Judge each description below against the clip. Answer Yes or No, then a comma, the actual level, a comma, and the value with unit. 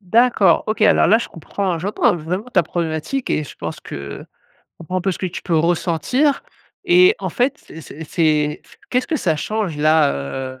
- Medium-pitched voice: Yes, medium, 175 Hz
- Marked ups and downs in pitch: Yes, wide, 5.8 semitones